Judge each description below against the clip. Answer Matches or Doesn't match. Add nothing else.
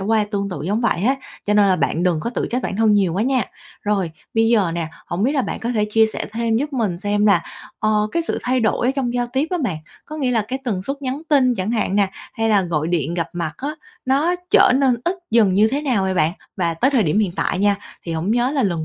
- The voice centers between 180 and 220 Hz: Matches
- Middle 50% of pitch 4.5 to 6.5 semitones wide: Matches